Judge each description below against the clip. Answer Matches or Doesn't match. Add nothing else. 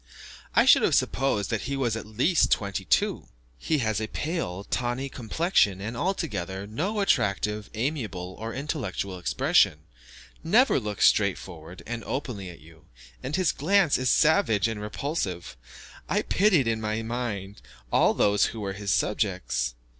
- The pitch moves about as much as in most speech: Doesn't match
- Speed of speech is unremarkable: Matches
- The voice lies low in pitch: Matches